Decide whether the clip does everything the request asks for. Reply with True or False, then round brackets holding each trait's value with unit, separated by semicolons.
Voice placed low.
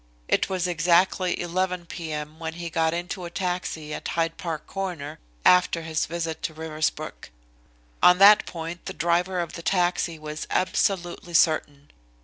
False (170 Hz)